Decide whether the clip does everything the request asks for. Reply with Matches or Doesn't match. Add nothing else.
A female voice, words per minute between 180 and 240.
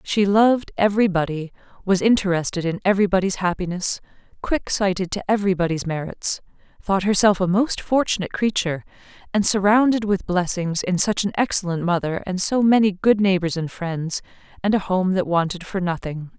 Doesn't match